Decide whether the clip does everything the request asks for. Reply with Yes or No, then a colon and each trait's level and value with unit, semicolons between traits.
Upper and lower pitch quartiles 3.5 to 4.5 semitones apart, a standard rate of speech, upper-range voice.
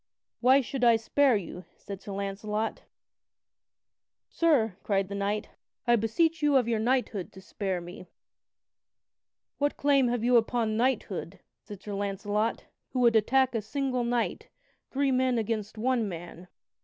Yes: average, 4.0 semitones; average, 145 wpm; high, 225 Hz